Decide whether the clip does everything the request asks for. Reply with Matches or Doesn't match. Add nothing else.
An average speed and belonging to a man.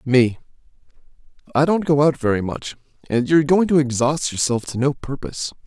Matches